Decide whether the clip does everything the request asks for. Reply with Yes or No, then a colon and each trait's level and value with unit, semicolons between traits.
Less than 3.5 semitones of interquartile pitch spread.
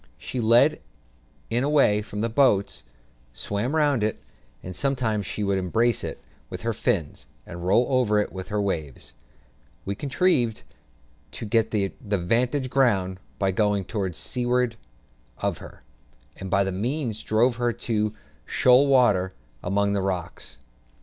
No: average, 4.2 semitones